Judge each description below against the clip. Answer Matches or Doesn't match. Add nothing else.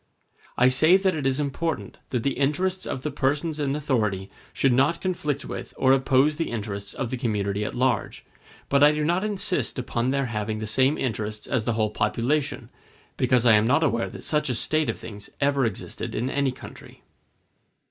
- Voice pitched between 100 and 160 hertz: Matches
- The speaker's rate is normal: Matches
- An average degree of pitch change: Matches